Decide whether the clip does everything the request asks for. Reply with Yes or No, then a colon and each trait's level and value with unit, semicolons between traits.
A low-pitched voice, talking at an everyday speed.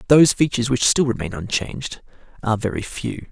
Yes: low, 125 Hz; average, 165 wpm